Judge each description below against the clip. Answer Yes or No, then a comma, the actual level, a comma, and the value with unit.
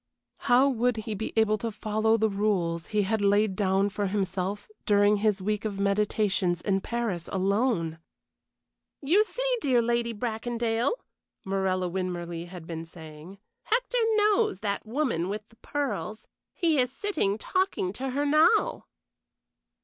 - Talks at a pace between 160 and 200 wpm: No, average, 140 wpm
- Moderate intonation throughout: Yes, average, 4.2 semitones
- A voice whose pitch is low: No, high, 210 Hz